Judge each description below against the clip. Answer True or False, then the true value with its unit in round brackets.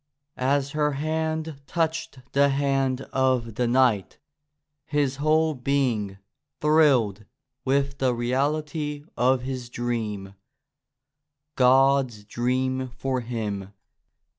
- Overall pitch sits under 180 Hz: True (135 Hz)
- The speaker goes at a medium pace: False (100 wpm)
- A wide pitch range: False (3.1 semitones)